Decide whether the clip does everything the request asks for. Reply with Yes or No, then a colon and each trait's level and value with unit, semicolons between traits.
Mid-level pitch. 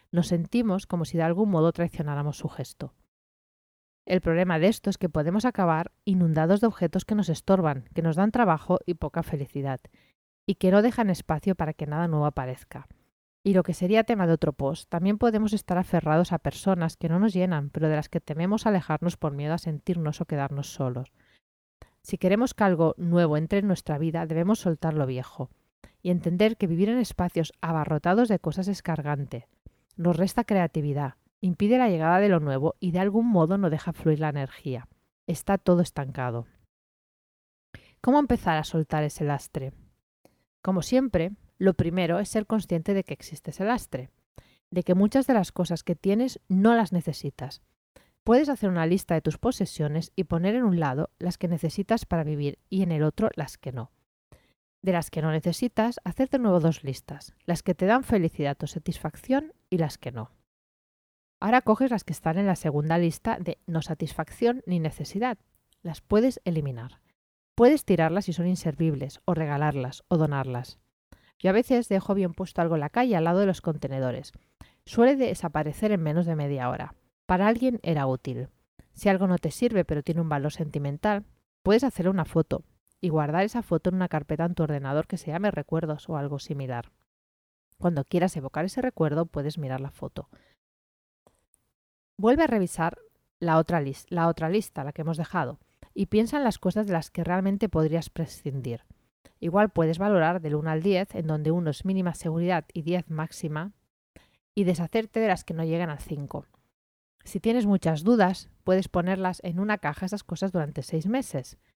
Yes: medium, 170 Hz